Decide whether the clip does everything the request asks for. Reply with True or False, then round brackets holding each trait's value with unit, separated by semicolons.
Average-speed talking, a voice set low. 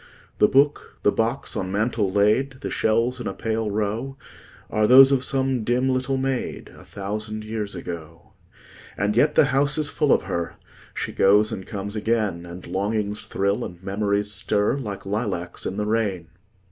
True (170 wpm; 105 Hz)